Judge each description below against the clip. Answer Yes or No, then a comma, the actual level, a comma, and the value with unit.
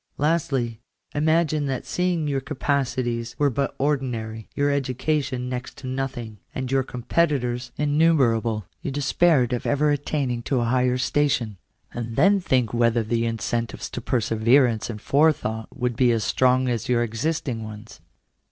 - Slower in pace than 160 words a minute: Yes, average, 150 wpm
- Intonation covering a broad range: No, average, 3.5 semitones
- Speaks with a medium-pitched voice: No, low, 125 Hz